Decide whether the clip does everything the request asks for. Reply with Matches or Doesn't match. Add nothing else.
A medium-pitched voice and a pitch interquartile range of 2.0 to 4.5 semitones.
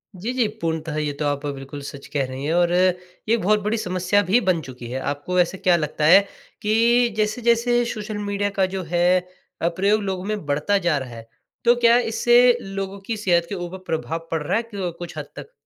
Doesn't match